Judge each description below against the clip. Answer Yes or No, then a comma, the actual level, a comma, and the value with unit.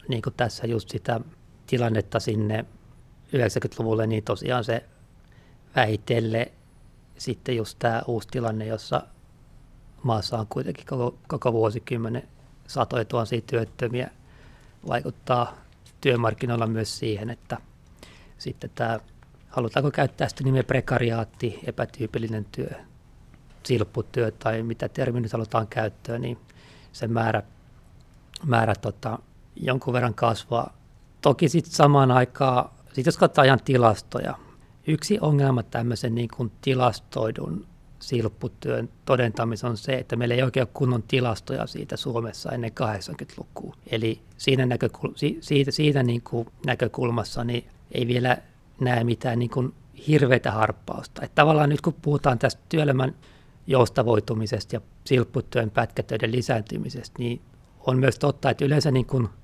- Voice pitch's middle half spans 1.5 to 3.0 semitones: Yes, narrow, 2.6 semitones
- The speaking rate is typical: Yes, average, 120 wpm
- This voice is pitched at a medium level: No, low, 120 Hz